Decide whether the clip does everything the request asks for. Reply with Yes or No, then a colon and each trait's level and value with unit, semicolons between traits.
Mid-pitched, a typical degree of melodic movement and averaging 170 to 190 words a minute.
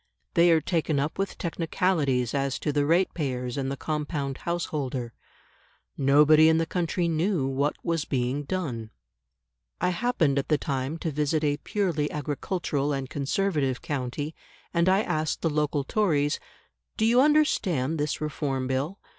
No: medium, 150 Hz; average, 3.6 semitones; average, 150 wpm